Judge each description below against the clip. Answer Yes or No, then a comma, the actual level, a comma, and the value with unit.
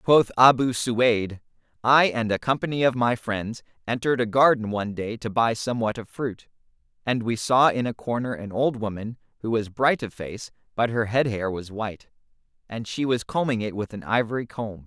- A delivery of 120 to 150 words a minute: No, average, 200 wpm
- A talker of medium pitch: No, low, 115 Hz